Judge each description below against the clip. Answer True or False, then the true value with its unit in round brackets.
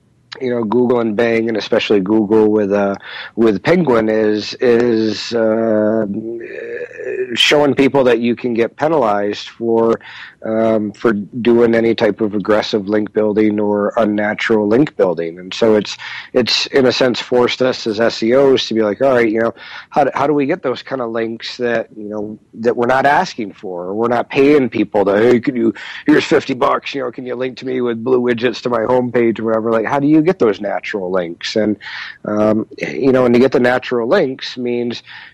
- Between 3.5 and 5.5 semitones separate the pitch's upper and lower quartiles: False (2.5 semitones)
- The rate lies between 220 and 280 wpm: False (200 wpm)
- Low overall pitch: True (115 Hz)